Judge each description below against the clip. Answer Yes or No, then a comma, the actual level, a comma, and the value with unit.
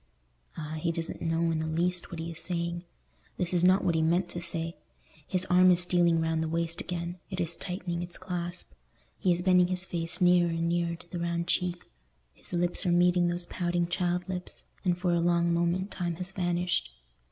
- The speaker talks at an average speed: No, fast, 210 wpm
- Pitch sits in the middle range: Yes, medium, 175 Hz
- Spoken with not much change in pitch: Yes, narrow, 1.0 semitones